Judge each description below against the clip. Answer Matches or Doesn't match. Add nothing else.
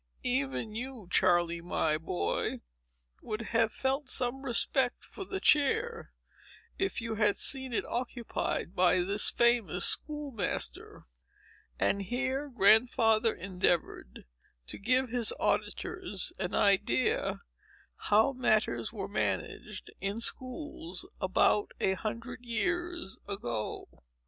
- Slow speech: Matches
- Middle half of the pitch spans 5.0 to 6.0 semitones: Matches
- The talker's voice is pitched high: Matches